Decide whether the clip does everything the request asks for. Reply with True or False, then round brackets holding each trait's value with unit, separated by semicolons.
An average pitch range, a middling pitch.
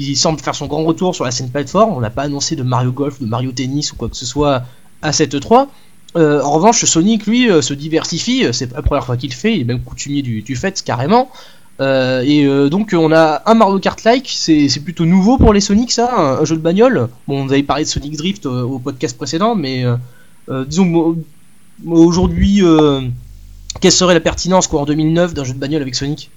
True (4.8 semitones; 155 Hz)